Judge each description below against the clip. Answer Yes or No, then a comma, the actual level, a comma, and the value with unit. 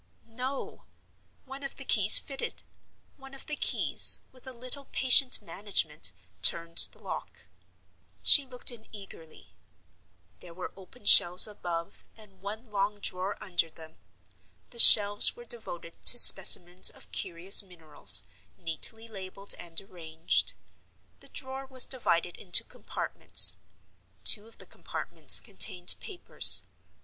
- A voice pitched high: Yes, high, 205 Hz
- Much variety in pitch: Yes, wide, 6.2 semitones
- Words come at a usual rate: No, slow, 130 wpm